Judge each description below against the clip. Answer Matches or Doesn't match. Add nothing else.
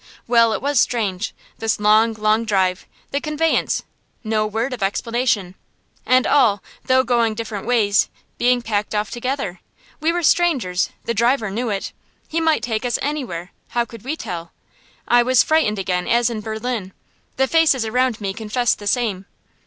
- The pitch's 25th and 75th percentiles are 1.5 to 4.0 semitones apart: Matches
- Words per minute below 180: Matches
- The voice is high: Matches